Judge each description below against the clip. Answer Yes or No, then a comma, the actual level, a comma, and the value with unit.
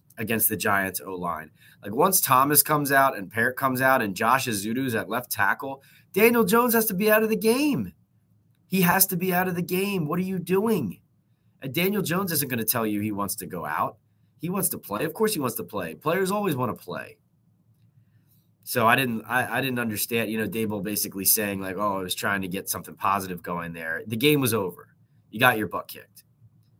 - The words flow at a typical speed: No, fast, 225 wpm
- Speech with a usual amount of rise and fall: No, wide, 9.0 semitones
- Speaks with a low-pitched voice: Yes, low, 130 Hz